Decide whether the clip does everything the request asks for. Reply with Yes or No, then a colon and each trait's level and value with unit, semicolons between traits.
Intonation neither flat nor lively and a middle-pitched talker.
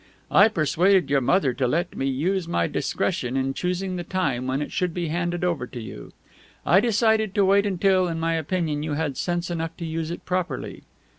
Yes: average, 4.1 semitones; medium, 170 Hz